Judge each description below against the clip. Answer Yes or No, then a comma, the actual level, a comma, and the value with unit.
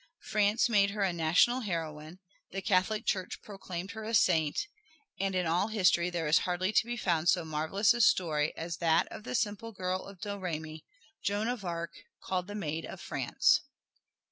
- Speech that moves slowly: No, average, 180 wpm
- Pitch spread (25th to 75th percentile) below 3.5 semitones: No, average, 3.8 semitones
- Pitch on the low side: No, medium, 185 Hz